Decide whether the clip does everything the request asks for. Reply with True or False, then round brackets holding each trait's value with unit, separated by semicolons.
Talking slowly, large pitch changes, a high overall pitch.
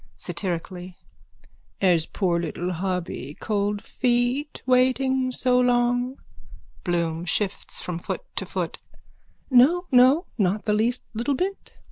True (115 wpm; 6.0 semitones; 220 Hz)